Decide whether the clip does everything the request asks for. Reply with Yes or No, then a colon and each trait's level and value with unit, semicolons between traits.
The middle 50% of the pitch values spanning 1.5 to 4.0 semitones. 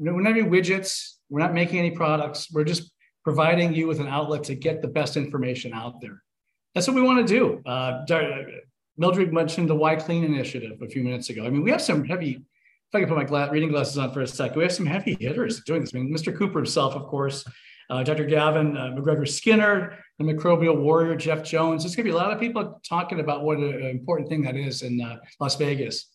Yes: average, 3.6 semitones